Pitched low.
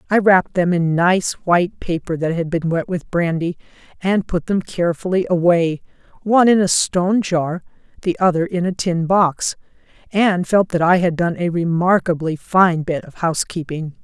No: medium, 175 Hz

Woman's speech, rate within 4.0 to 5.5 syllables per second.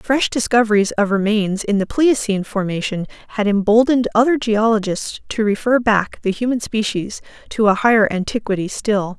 Yes: female; 5.2 syllables/s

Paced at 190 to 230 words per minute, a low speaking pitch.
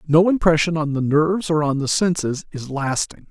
No: average, 200 wpm; medium, 155 Hz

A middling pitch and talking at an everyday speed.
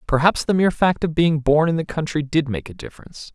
No: medium, 155 Hz; fast, 250 wpm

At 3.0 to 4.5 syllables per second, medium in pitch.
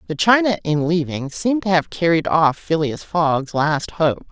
Yes: 4.4 syllables/s; medium, 165 Hz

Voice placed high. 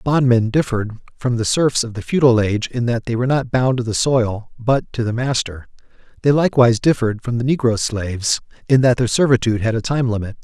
No: low, 120 Hz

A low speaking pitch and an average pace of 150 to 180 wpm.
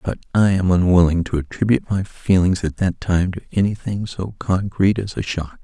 No: very low, 95 Hz; average, 190 wpm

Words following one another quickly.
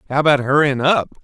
No: average, 195 wpm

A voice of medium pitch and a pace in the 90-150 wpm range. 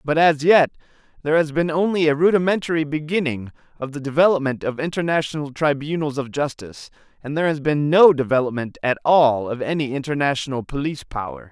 No: medium, 150 Hz; average, 160 wpm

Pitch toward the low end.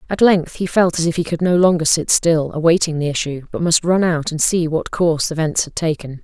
No: medium, 165 Hz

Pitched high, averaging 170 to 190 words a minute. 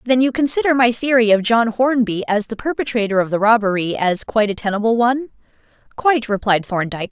Yes: high, 225 Hz; average, 185 wpm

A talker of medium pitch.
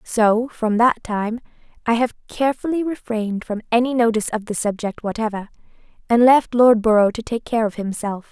No: high, 230 Hz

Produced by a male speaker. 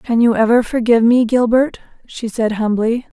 No: female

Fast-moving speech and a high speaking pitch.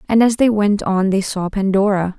Yes: fast, 220 wpm; high, 200 Hz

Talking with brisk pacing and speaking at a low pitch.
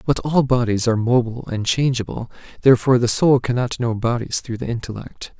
No: average, 180 wpm; low, 120 Hz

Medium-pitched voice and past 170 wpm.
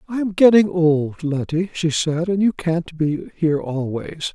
Yes: medium, 165 Hz; average, 180 wpm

